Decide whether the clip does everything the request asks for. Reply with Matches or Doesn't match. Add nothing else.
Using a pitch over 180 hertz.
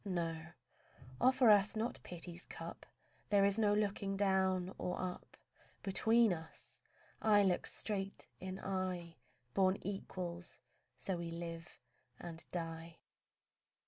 Matches